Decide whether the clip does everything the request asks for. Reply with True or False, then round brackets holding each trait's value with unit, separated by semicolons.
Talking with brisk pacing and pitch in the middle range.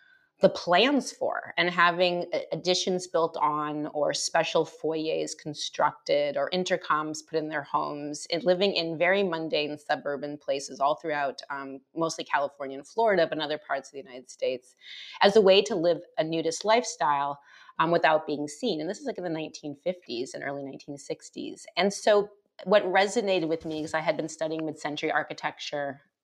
False (175 wpm; 160 Hz)